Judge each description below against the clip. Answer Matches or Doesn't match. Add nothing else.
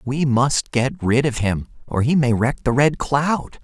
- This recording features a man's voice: Matches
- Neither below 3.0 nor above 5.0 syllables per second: Matches